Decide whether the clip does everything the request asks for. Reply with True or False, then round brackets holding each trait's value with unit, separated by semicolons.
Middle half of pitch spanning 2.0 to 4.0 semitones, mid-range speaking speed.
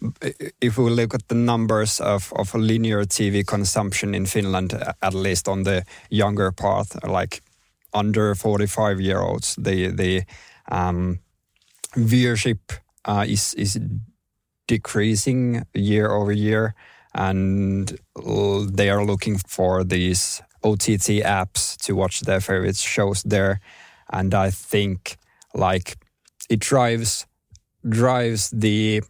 True (2.4 semitones; 120 wpm)